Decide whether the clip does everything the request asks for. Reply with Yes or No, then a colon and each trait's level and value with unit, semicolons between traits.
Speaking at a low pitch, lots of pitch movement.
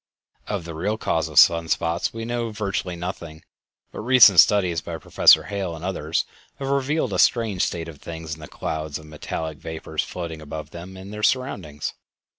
No: very low, 85 Hz; average, 4.7 semitones